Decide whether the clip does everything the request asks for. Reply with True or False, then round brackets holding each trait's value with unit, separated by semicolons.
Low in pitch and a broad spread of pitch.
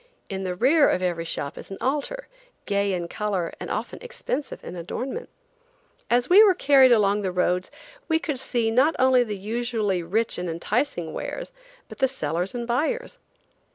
False (225 Hz; 6.8 semitones)